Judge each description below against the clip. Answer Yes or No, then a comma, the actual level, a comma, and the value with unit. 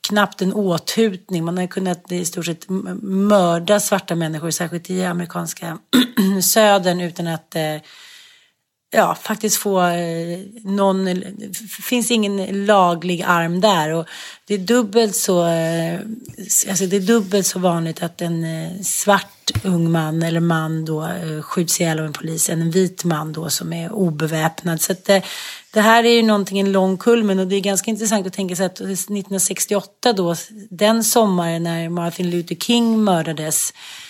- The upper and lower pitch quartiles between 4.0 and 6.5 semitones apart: No, average, 3.4 semitones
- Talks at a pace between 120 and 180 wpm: Yes, average, 155 wpm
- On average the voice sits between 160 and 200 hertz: Yes, medium, 185 Hz